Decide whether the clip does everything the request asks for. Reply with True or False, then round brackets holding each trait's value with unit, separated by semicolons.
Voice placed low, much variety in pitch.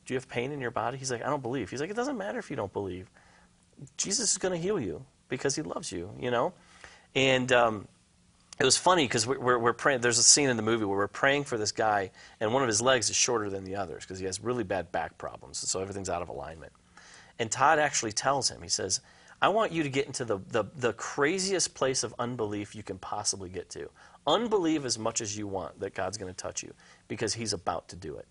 True (120 Hz; 6.0 semitones)